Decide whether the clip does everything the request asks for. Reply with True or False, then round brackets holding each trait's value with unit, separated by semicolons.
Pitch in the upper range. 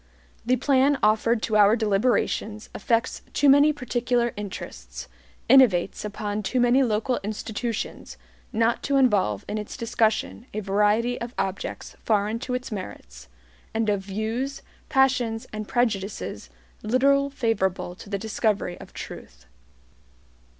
True (220 Hz)